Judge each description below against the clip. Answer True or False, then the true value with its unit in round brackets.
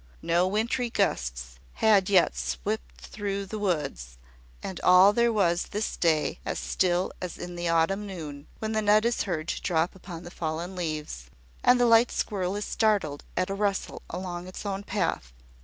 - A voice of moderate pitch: True (180 Hz)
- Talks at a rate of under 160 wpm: False (175 wpm)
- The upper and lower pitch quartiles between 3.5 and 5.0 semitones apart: True (4.5 semitones)